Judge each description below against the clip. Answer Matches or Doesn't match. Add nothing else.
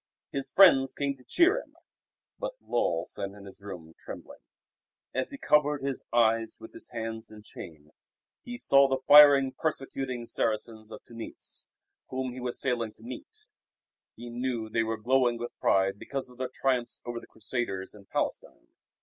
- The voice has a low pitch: Matches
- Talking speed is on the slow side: Doesn't match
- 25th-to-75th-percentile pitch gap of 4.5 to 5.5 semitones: Doesn't match